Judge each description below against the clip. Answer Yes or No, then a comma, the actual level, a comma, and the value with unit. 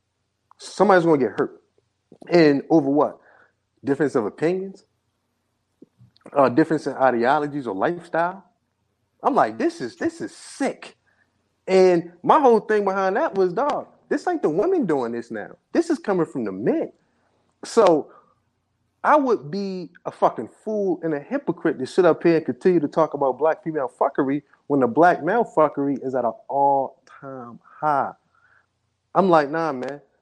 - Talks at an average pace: Yes, average, 160 wpm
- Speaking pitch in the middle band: Yes, medium, 160 Hz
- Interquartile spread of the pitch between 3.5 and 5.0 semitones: No, wide, 5.5 semitones